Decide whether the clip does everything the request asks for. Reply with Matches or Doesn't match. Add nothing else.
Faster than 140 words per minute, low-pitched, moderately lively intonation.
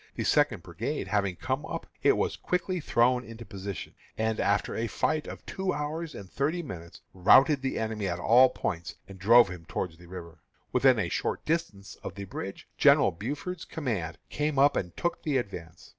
Doesn't match